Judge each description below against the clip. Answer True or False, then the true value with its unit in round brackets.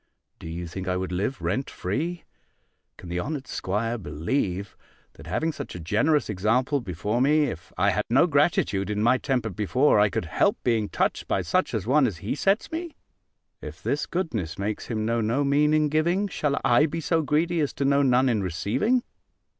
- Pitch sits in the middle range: False (125 Hz)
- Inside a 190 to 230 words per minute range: True (195 wpm)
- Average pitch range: False (7.0 semitones)